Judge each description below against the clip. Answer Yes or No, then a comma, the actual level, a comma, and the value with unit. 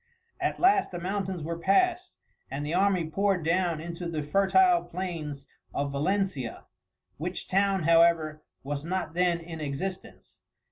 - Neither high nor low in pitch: Yes, medium, 175 Hz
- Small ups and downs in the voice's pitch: No, average, 3.7 semitones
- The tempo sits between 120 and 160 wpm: Yes, average, 140 wpm